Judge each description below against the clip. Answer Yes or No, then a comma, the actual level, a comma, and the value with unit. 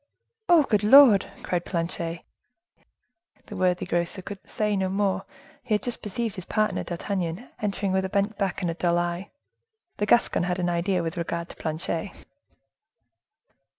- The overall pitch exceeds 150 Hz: Yes, high, 190 Hz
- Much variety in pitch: No, average, 3.2 semitones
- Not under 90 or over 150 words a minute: No, average, 160 wpm